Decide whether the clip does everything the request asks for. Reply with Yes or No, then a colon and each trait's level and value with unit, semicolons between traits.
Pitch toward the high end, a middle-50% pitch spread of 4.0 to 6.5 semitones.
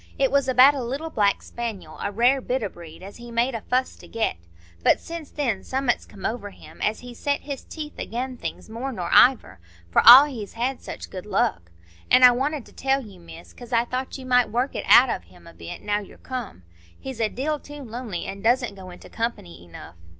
Yes: high, 240 Hz; average, 4.7 semitones